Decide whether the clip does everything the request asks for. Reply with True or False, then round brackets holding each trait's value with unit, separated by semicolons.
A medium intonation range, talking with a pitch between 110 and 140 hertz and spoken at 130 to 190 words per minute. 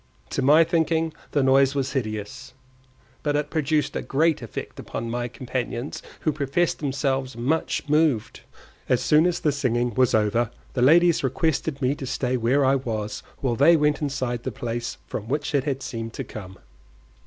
True (3.7 semitones; 135 Hz; 175 wpm)